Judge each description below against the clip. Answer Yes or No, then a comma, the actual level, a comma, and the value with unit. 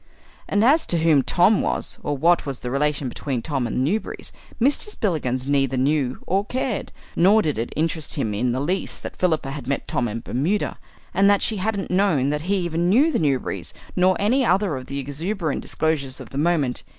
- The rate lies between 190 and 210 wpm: Yes, fast, 205 wpm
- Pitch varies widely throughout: Yes, wide, 6.1 semitones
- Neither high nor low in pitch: Yes, medium, 155 Hz